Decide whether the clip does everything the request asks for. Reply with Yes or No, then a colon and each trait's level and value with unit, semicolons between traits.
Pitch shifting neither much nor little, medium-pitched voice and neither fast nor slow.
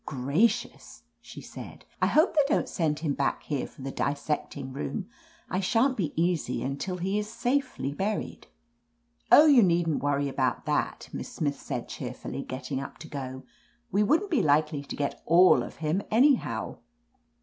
No: wide, 6.8 semitones; medium, 155 Hz; average, 170 wpm